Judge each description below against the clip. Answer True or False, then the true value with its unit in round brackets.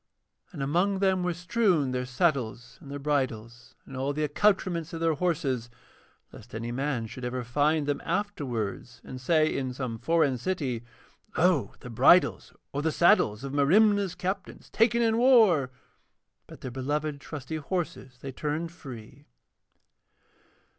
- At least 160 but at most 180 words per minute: False (145 wpm)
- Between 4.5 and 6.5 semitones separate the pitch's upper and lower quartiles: True (5.6 semitones)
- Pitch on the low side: False (145 Hz)